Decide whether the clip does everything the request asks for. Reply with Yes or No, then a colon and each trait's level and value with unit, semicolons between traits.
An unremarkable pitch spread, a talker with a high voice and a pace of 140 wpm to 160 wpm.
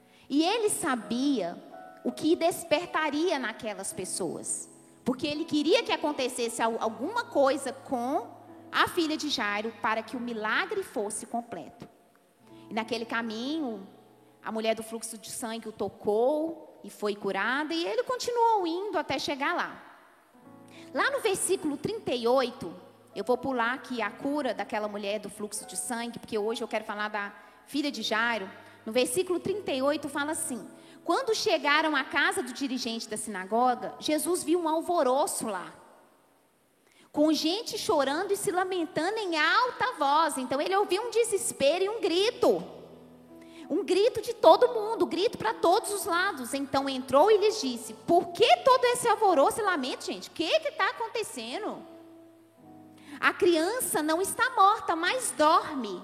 No: wide, 7.8 semitones; very high, 305 Hz; average, 150 wpm